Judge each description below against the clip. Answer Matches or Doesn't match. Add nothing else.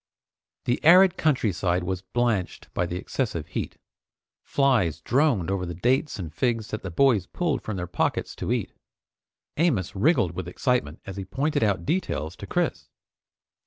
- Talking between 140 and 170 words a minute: Matches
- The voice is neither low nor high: Doesn't match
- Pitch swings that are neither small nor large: Doesn't match